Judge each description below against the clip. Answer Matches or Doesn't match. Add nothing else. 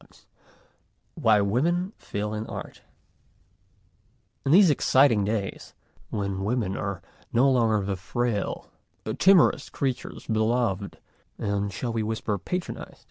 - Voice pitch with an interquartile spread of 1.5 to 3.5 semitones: Doesn't match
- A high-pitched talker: Doesn't match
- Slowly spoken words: Matches